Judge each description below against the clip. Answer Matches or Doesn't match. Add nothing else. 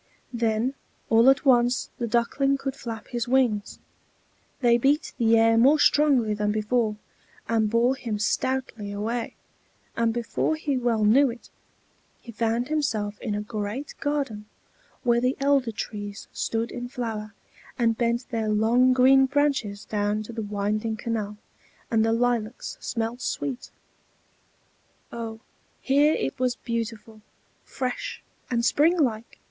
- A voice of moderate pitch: Doesn't match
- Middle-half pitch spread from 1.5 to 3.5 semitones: Matches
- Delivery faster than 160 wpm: Doesn't match